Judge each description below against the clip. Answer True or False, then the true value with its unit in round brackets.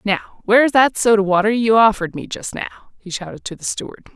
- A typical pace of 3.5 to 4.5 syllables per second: False (6.4 syllables/s)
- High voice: True (210 Hz)